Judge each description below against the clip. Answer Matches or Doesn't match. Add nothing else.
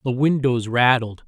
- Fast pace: Doesn't match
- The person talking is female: Doesn't match